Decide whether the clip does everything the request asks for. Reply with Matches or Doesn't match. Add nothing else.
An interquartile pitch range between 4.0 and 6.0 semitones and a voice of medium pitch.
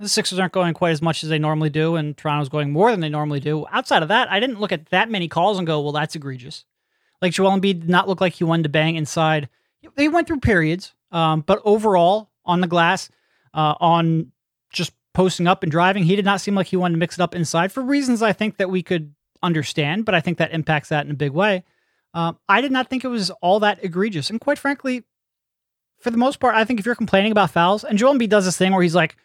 Matches